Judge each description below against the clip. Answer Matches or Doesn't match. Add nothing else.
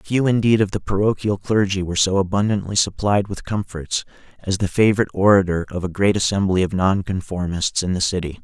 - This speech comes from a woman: Doesn't match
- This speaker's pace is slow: Doesn't match